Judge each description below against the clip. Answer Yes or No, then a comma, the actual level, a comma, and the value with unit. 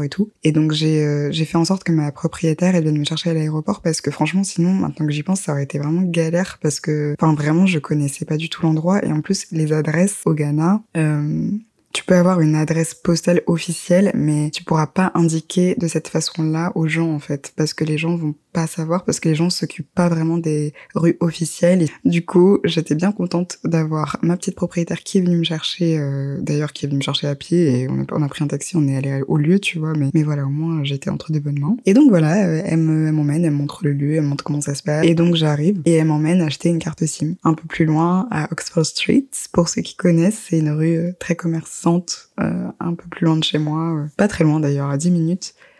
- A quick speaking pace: Yes, fast, 255 wpm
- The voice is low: No, medium, 160 Hz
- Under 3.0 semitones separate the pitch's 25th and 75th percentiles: Yes, narrow, 2.4 semitones